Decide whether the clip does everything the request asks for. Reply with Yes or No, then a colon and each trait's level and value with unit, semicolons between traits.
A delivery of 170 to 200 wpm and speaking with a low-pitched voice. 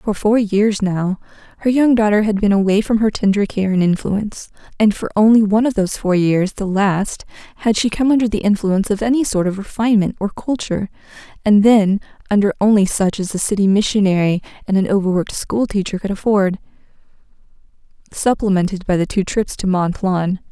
No: average, 175 wpm; high, 205 Hz